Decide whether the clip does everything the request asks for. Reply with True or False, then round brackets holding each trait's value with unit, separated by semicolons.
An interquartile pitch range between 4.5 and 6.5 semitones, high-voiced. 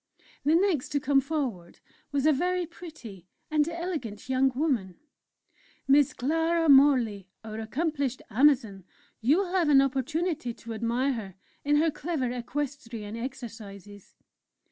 True (5.2 semitones; 270 Hz)